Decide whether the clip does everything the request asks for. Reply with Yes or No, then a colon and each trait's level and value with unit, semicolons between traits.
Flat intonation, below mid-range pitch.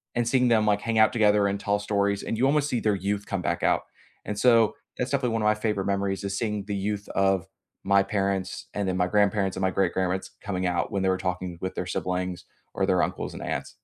Yes: narrow, 2.1 semitones; low, 100 Hz